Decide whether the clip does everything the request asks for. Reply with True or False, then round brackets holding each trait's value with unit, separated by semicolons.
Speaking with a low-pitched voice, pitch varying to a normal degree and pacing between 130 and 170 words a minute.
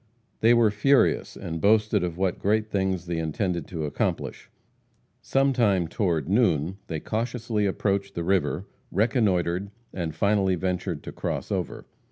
True (95 Hz; 3.8 semitones; 140 wpm)